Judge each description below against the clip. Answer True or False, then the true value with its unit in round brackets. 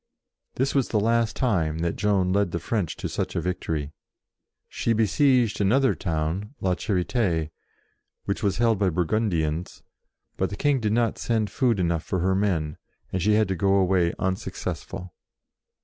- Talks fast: False (165 wpm)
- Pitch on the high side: False (95 Hz)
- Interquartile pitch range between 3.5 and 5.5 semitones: True (4.4 semitones)